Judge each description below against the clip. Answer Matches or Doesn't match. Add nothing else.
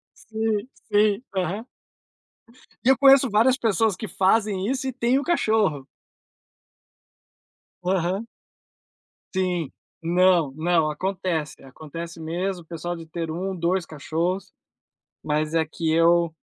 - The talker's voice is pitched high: Doesn't match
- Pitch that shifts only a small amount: Doesn't match